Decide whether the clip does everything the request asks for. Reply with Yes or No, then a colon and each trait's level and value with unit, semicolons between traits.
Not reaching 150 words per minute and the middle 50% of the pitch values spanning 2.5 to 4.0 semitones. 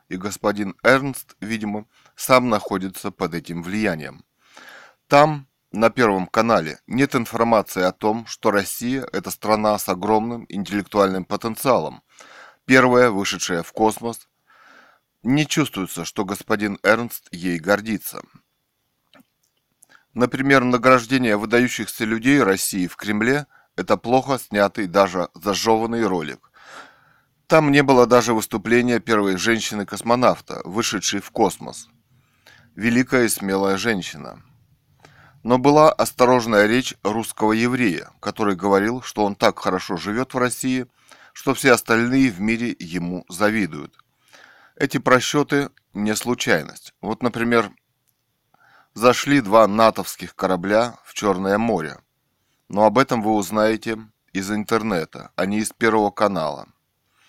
Yes: average, 115 wpm; average, 3.6 semitones